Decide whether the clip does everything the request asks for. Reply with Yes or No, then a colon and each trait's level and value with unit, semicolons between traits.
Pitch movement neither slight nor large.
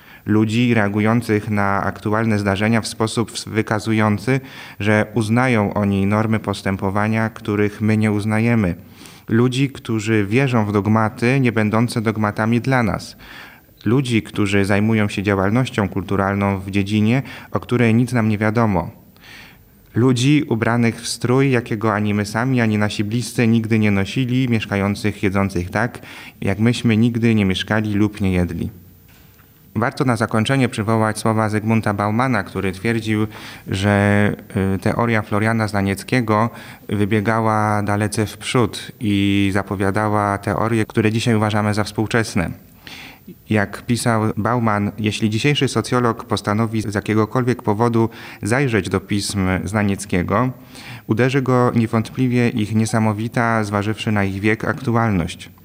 No: narrow, 2.1 semitones